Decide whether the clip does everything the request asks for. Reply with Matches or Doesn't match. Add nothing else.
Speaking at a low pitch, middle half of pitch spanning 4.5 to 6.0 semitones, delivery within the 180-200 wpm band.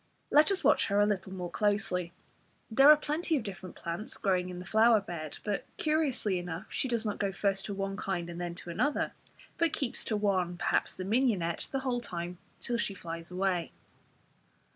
Doesn't match